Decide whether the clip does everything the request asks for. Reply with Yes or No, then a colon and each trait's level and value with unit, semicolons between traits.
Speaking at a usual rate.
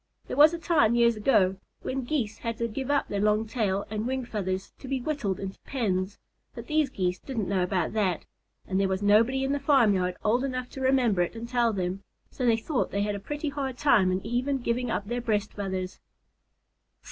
No: fast, 215 wpm